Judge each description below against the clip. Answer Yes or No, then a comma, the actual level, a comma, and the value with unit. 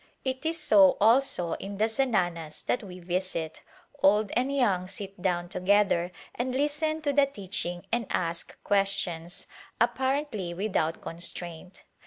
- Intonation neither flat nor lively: No, wide, 6.3 semitones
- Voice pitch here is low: No, high, 195 Hz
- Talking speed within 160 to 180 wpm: No, average, 140 wpm